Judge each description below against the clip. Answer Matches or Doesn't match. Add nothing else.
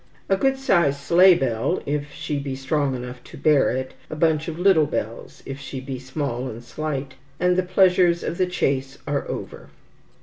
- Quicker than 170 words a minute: Matches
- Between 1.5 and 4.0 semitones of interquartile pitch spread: Doesn't match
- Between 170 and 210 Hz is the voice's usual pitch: Doesn't match